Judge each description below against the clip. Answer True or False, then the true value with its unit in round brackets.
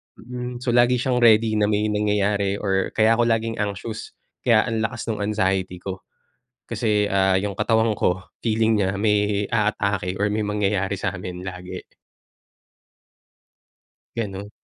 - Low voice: True (105 Hz)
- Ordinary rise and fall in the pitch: False (2.3 semitones)